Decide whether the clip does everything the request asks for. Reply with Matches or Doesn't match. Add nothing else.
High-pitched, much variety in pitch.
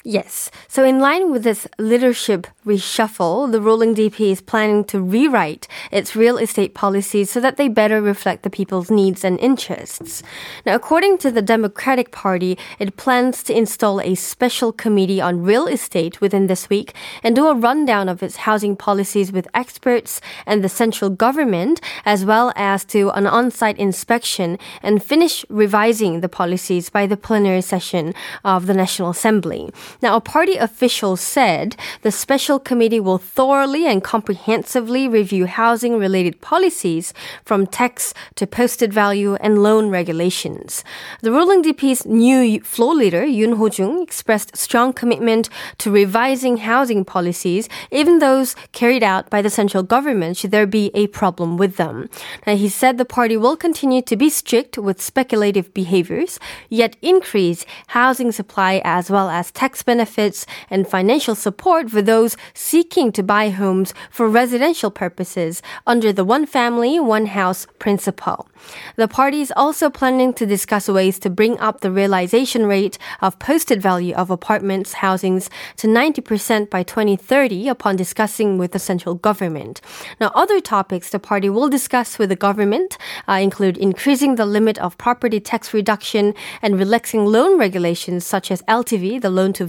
Doesn't match